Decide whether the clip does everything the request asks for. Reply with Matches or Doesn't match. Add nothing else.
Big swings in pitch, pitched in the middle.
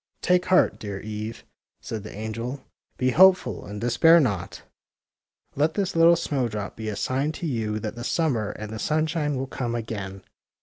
Doesn't match